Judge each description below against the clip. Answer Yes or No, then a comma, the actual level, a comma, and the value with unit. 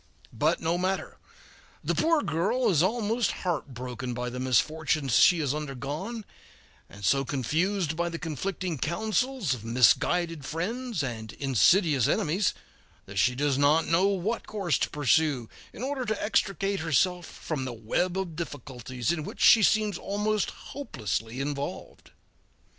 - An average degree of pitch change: No, wide, 6.8 semitones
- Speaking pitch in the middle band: Yes, medium, 160 Hz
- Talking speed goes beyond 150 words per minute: No, average, 140 wpm